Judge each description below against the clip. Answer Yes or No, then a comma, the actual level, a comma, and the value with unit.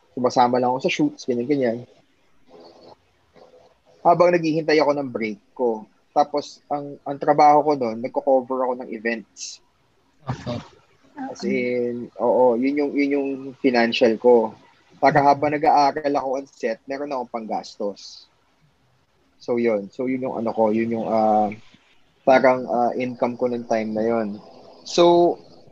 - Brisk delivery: No, average, 140 wpm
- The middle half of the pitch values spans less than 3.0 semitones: No, average, 3.7 semitones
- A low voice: Yes, low, 125 Hz